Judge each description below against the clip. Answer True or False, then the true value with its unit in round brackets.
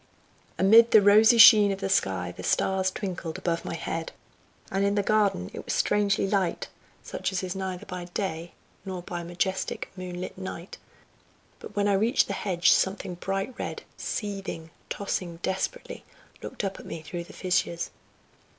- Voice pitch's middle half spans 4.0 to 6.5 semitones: False (2.5 semitones)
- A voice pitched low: False (190 Hz)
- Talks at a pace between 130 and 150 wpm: False (170 wpm)